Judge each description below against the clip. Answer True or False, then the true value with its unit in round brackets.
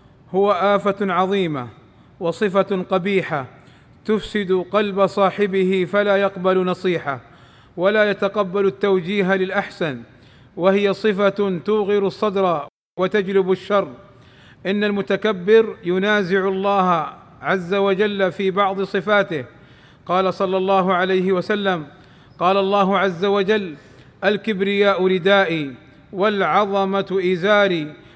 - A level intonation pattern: True (1.9 semitones)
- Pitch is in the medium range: False (195 Hz)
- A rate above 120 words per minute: False (90 wpm)